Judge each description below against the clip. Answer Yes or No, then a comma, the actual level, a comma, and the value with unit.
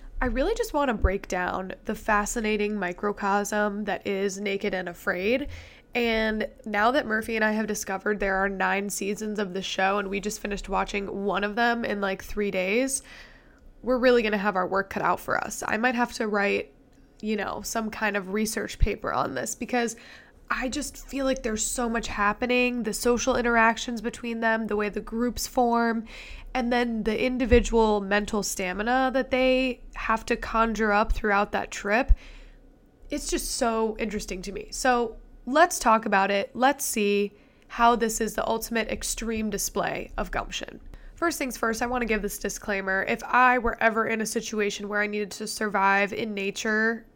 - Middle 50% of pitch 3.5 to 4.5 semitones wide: No, average, 2.9 semitones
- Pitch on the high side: Yes, high, 220 Hz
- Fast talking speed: No, average, 185 wpm